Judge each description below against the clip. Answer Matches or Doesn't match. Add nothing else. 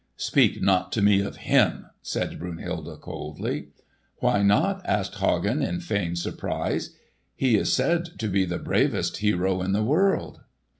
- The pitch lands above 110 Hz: Doesn't match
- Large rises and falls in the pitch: Matches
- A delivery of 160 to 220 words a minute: Doesn't match